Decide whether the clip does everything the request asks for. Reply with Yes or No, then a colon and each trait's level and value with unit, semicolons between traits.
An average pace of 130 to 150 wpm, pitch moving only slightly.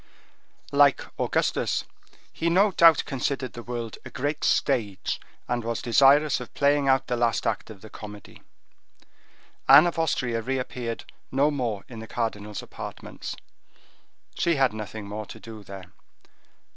No: average, 145 wpm; average, 4.3 semitones